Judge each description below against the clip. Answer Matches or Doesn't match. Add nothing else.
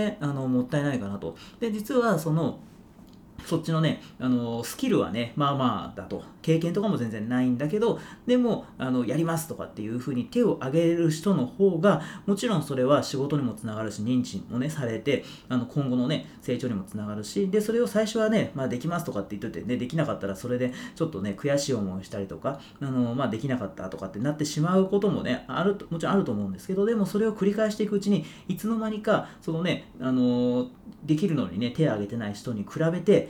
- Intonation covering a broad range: Matches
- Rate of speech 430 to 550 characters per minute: Matches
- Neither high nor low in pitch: Matches